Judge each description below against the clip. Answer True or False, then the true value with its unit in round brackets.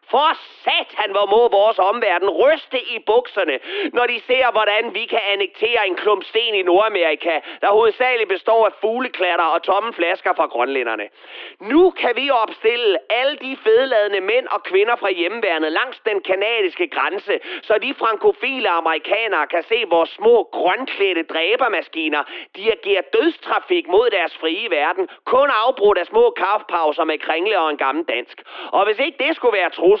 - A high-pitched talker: True (285 Hz)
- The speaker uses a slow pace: False (165 wpm)